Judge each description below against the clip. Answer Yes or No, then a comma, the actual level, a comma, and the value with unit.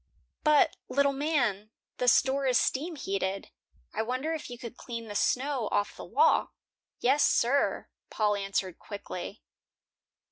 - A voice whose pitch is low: No, high, 245 Hz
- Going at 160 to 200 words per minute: No, average, 140 wpm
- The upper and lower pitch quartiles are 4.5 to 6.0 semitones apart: Yes, average, 5.3 semitones